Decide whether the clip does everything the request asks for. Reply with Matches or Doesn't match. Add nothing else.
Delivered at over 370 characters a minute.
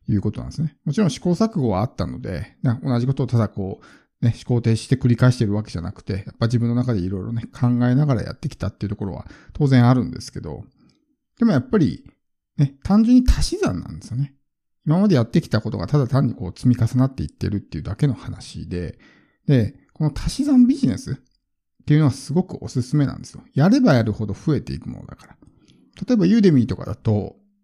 Matches